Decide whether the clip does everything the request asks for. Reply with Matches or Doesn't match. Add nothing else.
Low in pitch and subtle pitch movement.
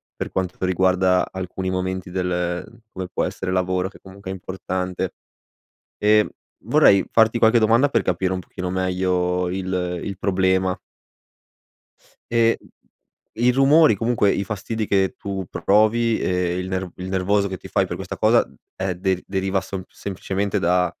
Matches